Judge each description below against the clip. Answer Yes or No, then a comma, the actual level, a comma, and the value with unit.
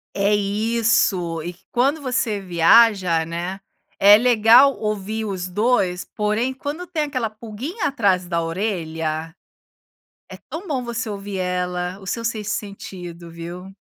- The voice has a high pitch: Yes, high, 205 Hz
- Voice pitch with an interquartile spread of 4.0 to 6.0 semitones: Yes, average, 4.6 semitones